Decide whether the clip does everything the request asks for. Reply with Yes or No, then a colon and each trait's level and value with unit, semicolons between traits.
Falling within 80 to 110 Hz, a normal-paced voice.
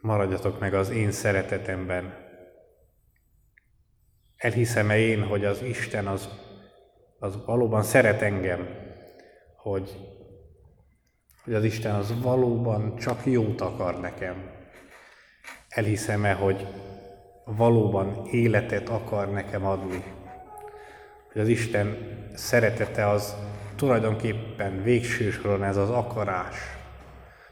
No: low, 105 Hz; slow, 90 wpm